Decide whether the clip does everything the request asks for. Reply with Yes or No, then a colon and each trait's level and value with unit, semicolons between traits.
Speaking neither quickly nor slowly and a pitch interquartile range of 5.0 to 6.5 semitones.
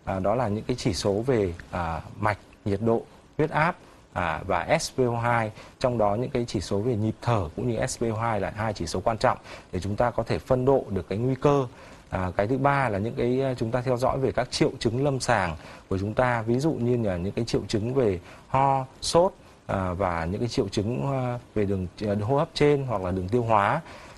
No: average, 230 wpm; average, 4.2 semitones